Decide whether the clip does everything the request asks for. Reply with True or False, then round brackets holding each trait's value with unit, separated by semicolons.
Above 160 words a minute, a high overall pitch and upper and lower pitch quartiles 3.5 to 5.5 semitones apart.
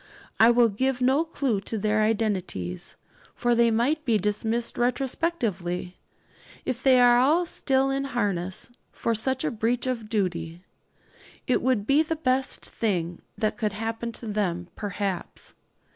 False (145 wpm; 230 Hz; 4.1 semitones)